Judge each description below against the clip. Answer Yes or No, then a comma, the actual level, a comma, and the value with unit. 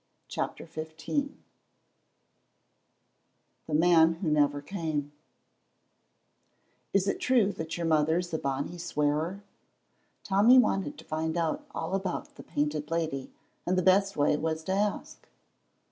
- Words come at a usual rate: No, slow, 125 wpm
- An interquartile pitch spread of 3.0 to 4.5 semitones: Yes, average, 3.7 semitones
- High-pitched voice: No, medium, 160 Hz